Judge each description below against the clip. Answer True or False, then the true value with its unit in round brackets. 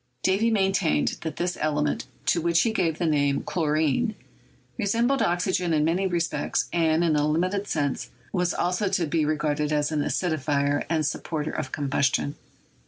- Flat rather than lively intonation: False (3.5 semitones)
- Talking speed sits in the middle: True (165 wpm)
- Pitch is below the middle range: False (160 Hz)